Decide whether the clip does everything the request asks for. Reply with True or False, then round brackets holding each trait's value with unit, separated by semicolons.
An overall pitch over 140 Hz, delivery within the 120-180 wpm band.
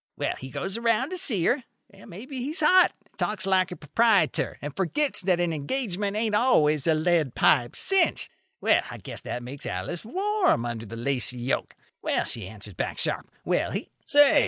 False (185 Hz; 190 wpm)